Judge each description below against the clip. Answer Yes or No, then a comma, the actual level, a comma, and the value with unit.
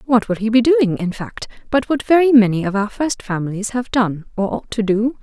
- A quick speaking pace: Yes, fast, 240 wpm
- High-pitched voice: Yes, high, 225 Hz